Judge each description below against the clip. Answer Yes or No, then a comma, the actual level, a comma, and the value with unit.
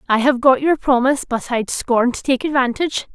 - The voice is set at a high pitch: Yes, very high, 260 Hz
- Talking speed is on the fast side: Yes, fast, 210 wpm